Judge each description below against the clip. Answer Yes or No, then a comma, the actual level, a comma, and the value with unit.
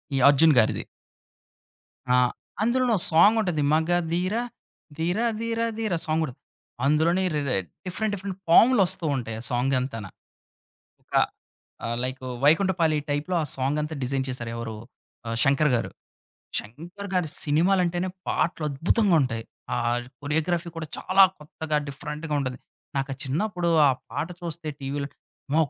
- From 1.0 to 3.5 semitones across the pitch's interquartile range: No, average, 4.7 semitones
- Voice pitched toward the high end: No, medium, 160 Hz